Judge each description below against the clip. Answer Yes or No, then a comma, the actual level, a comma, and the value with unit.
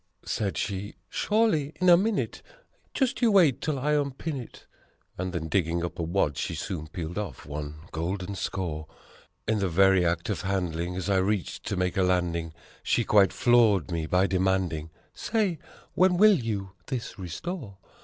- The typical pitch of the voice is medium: No, very low, 95 Hz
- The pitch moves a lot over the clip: Yes, wide, 7.3 semitones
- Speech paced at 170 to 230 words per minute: Yes, average, 175 wpm